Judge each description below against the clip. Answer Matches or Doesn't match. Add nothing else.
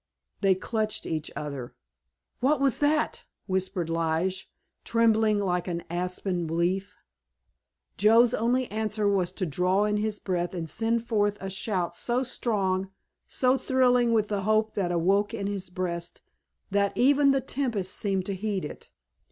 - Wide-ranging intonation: Doesn't match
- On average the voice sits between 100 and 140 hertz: Doesn't match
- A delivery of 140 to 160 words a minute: Matches